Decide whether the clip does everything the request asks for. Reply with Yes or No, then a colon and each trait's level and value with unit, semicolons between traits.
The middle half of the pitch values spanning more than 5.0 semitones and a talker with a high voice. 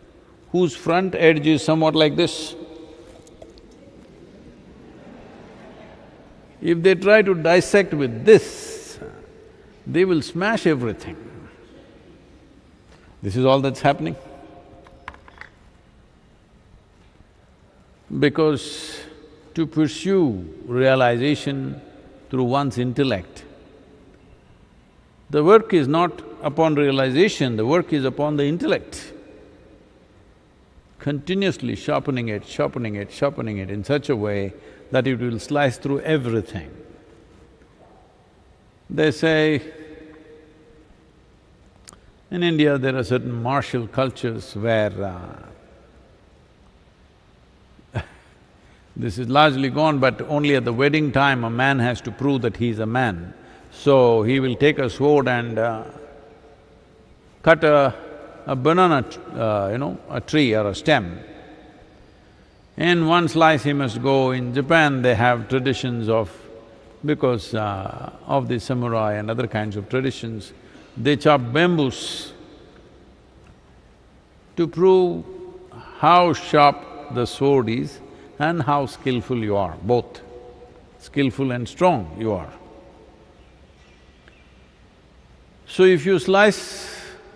No: wide, 5.6 semitones; low, 135 Hz